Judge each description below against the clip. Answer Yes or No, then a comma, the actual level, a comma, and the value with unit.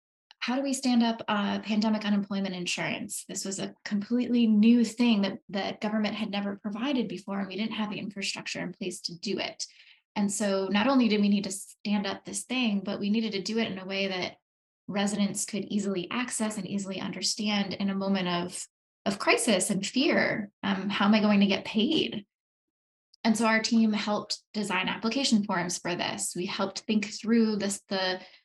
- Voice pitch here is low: No, high, 205 Hz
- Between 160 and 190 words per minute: No, average, 200 wpm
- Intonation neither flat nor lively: No, narrow, 2.1 semitones